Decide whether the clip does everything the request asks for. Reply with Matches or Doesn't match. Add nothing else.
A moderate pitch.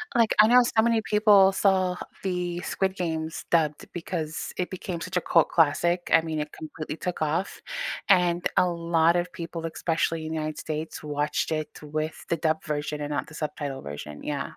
Matches